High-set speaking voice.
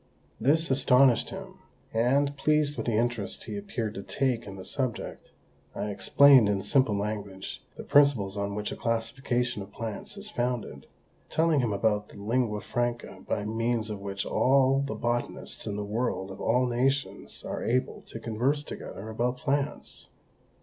No: low, 120 Hz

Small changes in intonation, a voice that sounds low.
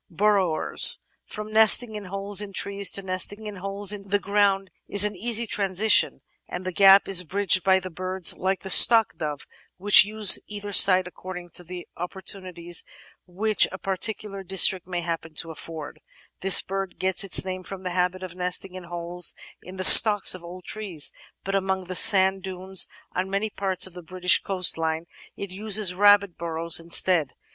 No: narrow, 2.0 semitones; high, 190 Hz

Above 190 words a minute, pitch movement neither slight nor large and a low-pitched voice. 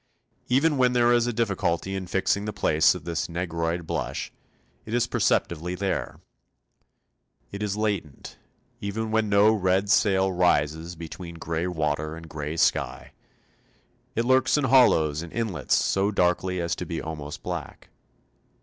No: average, 150 wpm; average, 4.6 semitones; very low, 95 Hz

